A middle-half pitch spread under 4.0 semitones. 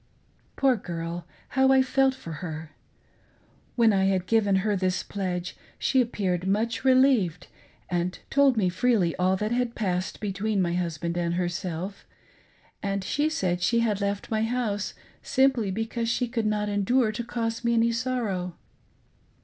No: average, 4.6 semitones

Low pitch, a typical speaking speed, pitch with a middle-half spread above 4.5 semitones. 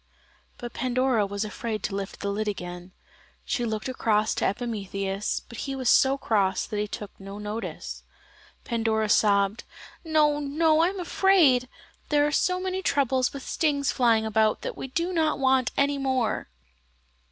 No: high, 240 Hz; average, 165 wpm; average, 5.1 semitones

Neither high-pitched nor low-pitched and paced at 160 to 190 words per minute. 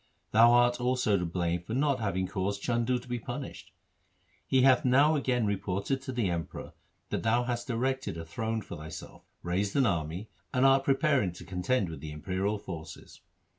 No: low, 110 Hz; average, 180 wpm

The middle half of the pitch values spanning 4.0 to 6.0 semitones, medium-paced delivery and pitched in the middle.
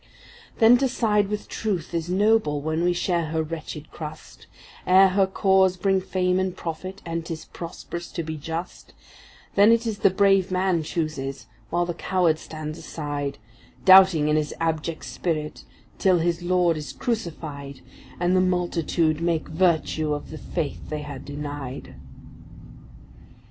No: average, 3.2 semitones; average, 150 wpm; medium, 170 Hz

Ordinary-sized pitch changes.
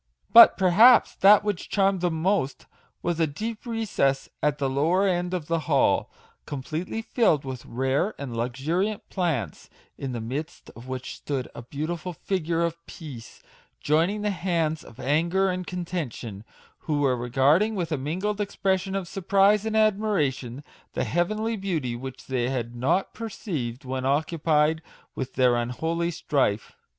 No: wide, 6.3 semitones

